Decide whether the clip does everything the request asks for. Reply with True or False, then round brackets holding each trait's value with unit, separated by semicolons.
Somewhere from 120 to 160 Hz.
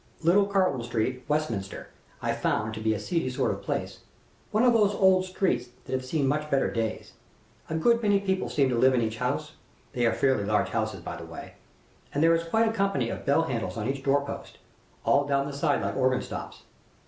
True (140 Hz)